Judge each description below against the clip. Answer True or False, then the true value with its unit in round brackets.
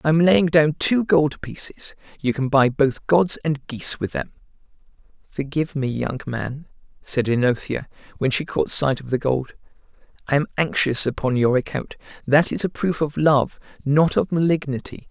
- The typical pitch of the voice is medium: True (145 Hz)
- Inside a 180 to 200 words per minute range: False (170 wpm)